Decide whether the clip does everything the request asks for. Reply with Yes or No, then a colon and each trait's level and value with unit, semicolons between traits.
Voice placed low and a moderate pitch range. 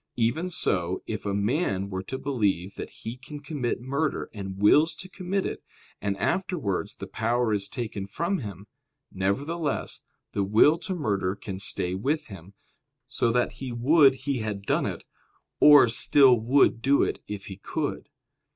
No: low, 120 Hz; wide, 6.5 semitones